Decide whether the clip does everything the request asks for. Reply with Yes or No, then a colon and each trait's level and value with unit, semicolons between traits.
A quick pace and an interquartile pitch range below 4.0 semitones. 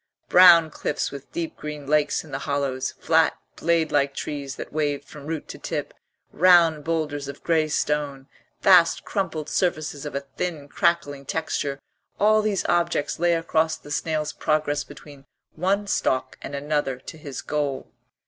No: average, 160 wpm; narrow, 2.6 semitones